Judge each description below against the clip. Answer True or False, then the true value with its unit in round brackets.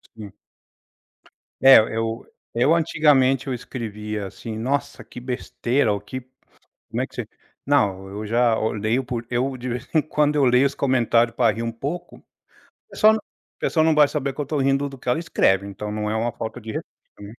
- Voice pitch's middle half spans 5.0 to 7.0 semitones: False (4.0 semitones)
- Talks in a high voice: False (125 Hz)